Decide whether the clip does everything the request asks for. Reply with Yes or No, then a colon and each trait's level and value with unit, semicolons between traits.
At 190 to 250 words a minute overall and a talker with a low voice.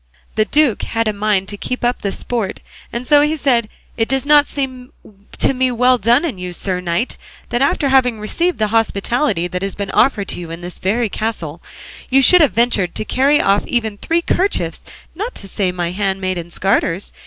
No: average, 195 wpm; high, 225 Hz